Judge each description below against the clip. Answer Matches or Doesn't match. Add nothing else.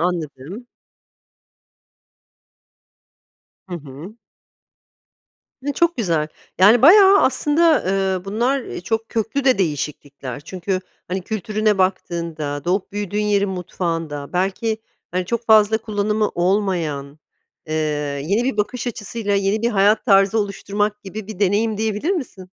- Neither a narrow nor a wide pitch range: Matches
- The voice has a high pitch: Matches